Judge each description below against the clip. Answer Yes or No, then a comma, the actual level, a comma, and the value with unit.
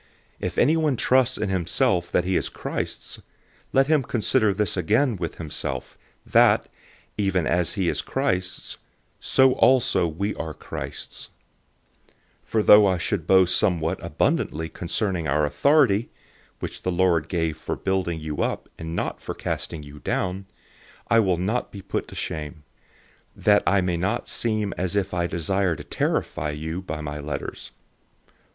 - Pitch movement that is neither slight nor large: Yes, average, 4.1 semitones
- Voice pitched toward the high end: No, very low, 90 Hz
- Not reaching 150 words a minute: No, average, 155 wpm